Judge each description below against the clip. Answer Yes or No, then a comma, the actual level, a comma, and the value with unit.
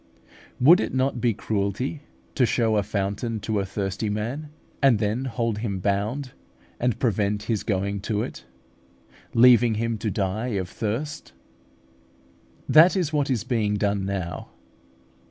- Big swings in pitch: No, average, 3.8 semitones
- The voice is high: No, low, 110 Hz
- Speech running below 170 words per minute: Yes, average, 145 wpm